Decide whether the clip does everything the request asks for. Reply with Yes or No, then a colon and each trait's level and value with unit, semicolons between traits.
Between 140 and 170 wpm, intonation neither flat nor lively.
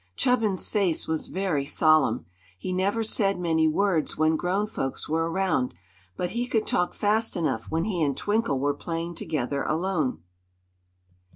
Yes: average, 155 wpm; average, 4.3 semitones